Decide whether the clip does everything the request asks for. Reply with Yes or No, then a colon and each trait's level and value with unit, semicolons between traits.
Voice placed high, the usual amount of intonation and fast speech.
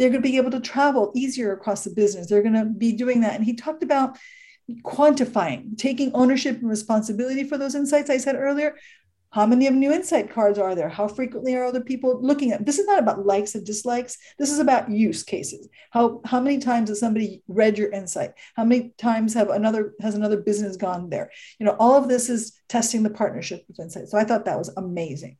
Yes: high, 230 Hz; average, 4.0 semitones; fast, 225 wpm